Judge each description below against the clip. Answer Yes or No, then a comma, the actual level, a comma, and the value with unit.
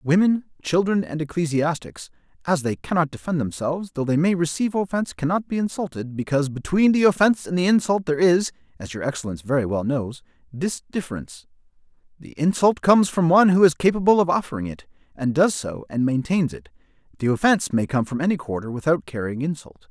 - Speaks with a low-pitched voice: No, medium, 155 Hz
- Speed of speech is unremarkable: Yes, average, 185 wpm